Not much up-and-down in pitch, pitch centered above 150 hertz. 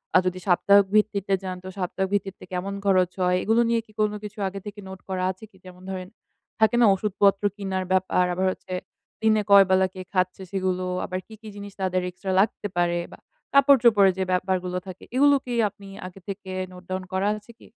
Yes: narrow, 1.9 semitones; high, 190 Hz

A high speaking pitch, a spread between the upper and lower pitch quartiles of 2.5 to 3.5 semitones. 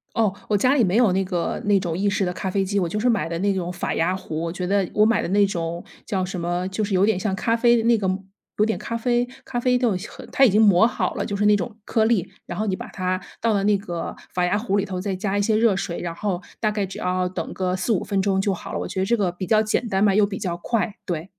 Yes: high, 200 Hz; average, 2.8 semitones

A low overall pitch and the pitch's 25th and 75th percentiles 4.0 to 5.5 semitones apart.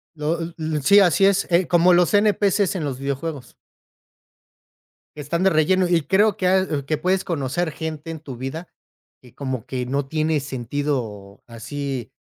No: medium, 155 Hz; average, 4.6 semitones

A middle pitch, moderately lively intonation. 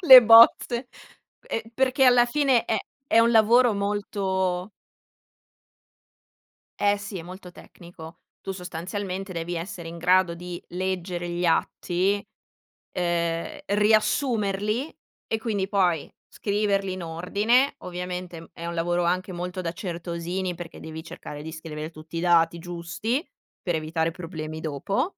Yes: medium, 180 Hz; average, 3.4 semitones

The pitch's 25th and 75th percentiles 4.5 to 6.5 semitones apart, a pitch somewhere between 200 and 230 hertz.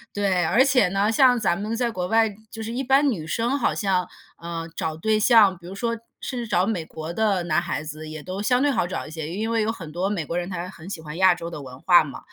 No: average, 5.0 semitones; high, 190 Hz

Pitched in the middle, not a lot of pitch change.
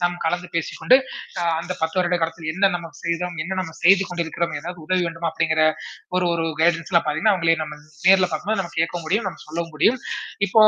Yes: medium, 170 Hz; narrow, 1.9 semitones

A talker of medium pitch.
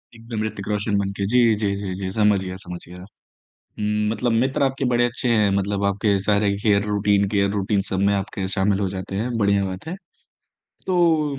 No: low, 105 Hz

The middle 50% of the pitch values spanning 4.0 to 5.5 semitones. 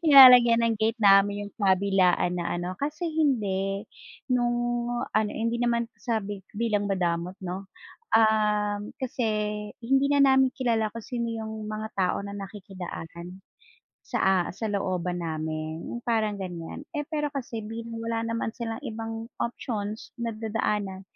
No: average, 3.3 semitones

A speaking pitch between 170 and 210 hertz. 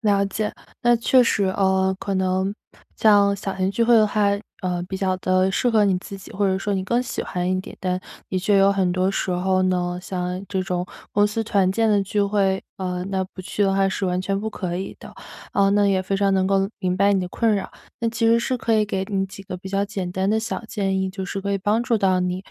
Yes: high, 195 Hz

